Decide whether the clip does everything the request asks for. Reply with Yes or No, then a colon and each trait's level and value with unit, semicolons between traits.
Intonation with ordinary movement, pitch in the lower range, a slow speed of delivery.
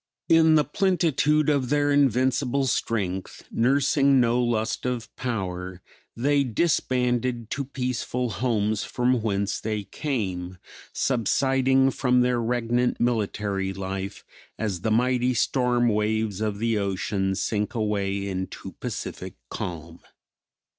Yes: average, 4.2 semitones; low, 120 Hz; slow, 115 wpm